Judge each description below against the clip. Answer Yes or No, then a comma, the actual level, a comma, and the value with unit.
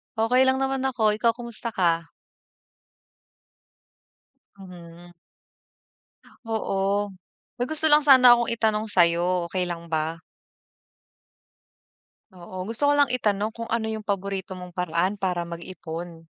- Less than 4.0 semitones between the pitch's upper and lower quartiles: No, average, 5.0 semitones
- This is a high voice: Yes, high, 195 Hz